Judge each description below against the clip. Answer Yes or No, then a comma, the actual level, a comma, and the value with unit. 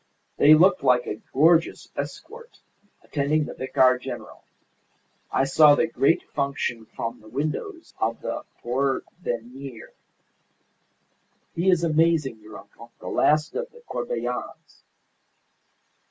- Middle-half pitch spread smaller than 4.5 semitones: No, average, 5.0 semitones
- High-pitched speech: No, medium, 140 Hz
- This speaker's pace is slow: Yes, slow, 115 wpm